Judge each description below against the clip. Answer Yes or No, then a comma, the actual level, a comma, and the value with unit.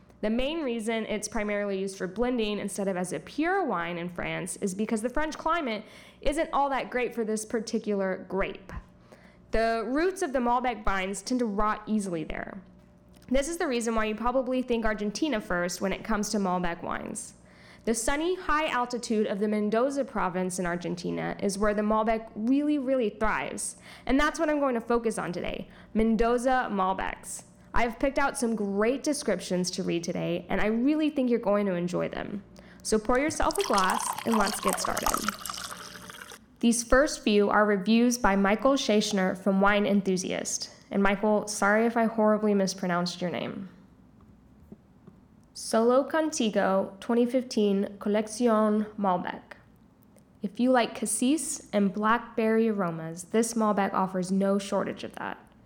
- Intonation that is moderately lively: Yes, average, 3.9 semitones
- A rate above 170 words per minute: No, average, 160 wpm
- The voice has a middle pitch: No, high, 215 Hz